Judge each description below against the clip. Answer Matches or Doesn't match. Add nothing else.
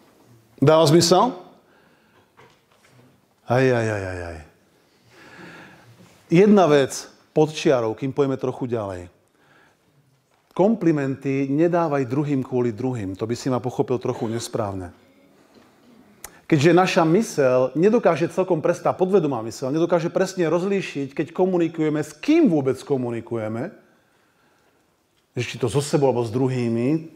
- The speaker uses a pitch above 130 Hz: Matches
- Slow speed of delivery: Matches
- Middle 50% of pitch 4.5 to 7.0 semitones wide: Matches